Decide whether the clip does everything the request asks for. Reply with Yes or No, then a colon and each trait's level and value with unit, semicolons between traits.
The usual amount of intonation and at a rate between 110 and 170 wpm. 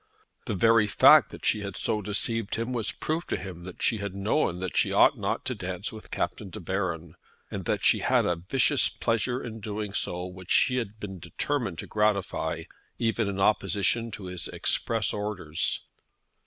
No: average, 3.5 semitones; average, 185 wpm